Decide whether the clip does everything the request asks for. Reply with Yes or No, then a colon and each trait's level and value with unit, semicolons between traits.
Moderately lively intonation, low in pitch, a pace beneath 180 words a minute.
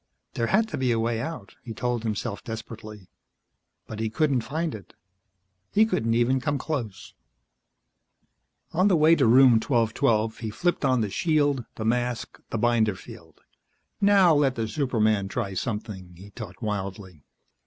Yes: average, 4.3 semitones; low, 115 Hz; average, 155 wpm